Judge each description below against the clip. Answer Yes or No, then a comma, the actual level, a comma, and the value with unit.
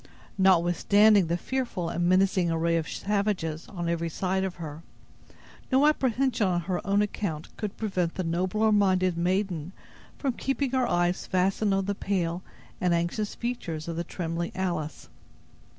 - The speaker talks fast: No, average, 150 wpm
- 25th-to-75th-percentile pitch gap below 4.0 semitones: Yes, average, 3.4 semitones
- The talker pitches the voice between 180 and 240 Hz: Yes, medium, 185 Hz